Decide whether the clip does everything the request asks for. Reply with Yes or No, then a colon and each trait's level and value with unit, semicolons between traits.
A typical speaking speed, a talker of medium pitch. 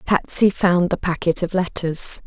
Yes: average, 160 wpm; medium, 180 Hz